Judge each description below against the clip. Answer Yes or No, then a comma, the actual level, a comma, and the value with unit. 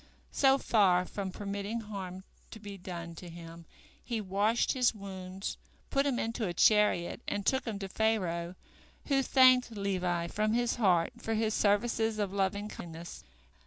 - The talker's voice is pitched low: No, high, 200 Hz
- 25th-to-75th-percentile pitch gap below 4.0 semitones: Yes, average, 3.5 semitones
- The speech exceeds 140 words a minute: Yes, average, 160 wpm